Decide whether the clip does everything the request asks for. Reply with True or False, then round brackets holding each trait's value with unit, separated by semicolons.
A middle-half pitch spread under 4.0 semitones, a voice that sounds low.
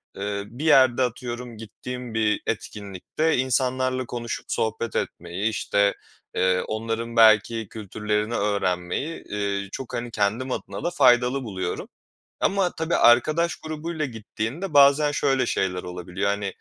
False (4.3 semitones; 115 Hz)